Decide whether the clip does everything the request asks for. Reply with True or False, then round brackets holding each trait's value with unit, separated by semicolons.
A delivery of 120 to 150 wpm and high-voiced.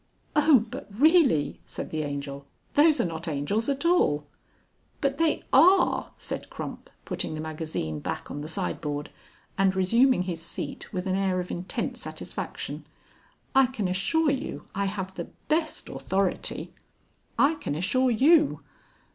True (145 wpm; 195 Hz)